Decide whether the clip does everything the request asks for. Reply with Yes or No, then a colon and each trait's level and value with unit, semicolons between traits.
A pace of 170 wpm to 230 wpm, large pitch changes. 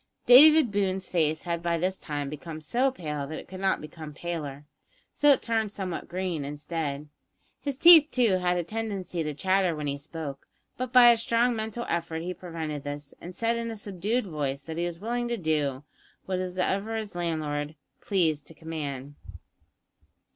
Yes: average, 175 wpm; wide, 6.1 semitones